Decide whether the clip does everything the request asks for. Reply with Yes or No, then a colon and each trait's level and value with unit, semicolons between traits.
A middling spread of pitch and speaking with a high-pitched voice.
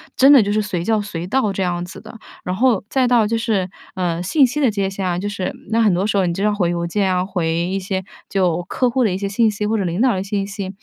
Yes: average, 3.3 semitones; high, 200 Hz